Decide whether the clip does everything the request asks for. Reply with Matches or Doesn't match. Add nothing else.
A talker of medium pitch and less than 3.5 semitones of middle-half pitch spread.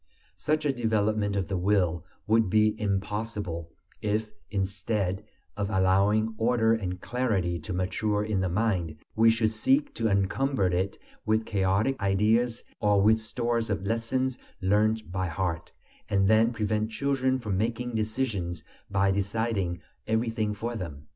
Doesn't match